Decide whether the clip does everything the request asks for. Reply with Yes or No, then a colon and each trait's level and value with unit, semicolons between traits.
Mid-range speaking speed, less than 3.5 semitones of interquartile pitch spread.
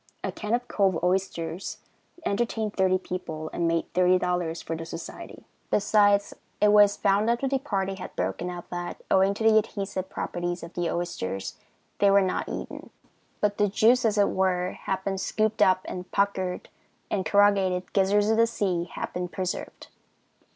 Yes: average, 170 wpm; narrow, 2.5 semitones